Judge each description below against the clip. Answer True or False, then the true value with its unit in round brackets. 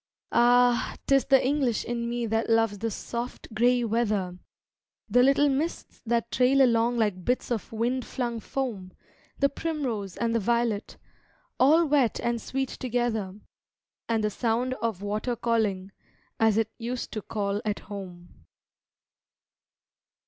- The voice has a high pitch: True (235 Hz)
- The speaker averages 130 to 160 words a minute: True (140 wpm)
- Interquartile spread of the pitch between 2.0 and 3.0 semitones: True (2.6 semitones)